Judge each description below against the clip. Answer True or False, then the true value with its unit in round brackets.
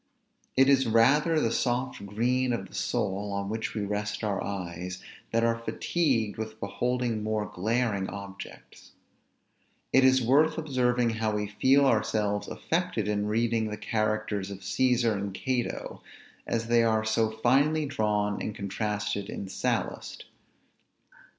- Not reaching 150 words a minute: True (140 wpm)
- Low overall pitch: True (110 Hz)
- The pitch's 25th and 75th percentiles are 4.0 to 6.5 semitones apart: False (3.2 semitones)